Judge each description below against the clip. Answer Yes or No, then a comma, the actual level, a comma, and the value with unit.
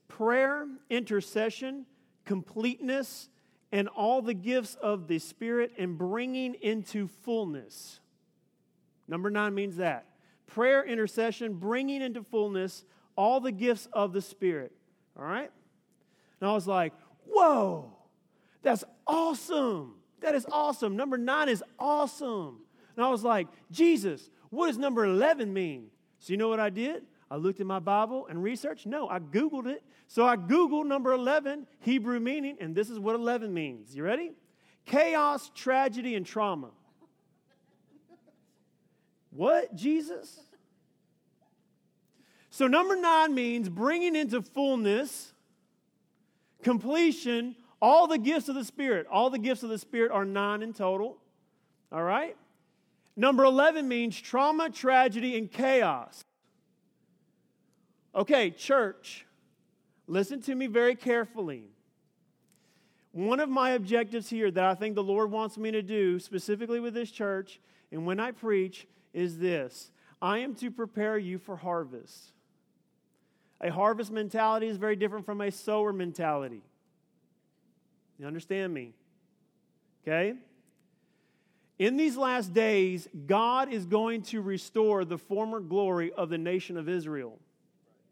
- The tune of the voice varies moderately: Yes, average, 4.9 semitones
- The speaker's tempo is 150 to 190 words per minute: No, slow, 135 wpm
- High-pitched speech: Yes, high, 220 Hz